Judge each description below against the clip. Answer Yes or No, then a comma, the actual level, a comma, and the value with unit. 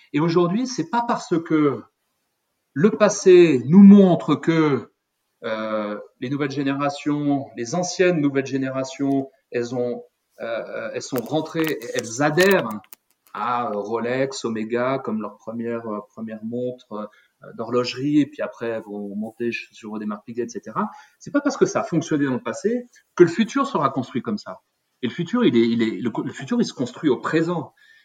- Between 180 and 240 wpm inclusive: No, average, 170 wpm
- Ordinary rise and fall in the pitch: No, wide, 7.1 semitones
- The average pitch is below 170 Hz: Yes, medium, 140 Hz